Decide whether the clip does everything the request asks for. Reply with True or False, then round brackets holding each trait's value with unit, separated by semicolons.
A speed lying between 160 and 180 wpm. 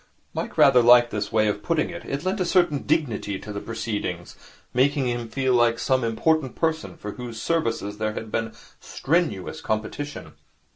True (175 wpm)